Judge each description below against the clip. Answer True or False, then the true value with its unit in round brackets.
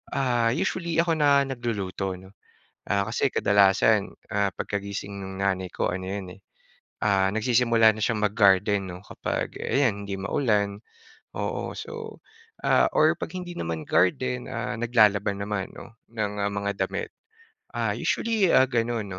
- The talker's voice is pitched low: True (105 Hz)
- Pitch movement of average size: True (3.4 semitones)